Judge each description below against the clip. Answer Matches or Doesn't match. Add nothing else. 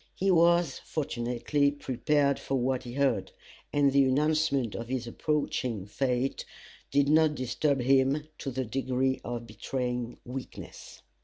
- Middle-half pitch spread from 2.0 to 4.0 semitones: Matches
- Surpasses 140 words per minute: Doesn't match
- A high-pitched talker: Doesn't match